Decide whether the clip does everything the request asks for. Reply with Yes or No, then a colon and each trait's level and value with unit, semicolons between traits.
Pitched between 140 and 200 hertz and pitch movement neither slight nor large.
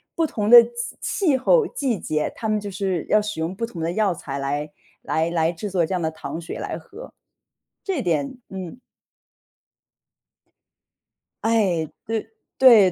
No: high, 195 Hz; wide, 5.9 semitones